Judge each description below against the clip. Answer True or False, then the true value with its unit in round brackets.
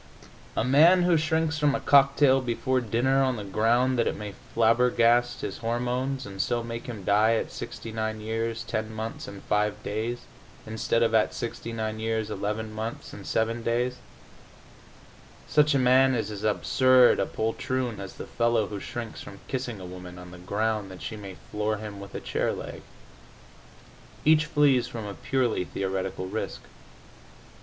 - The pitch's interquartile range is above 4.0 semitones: False (3.2 semitones)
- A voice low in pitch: True (115 Hz)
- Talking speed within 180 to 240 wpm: False (165 wpm)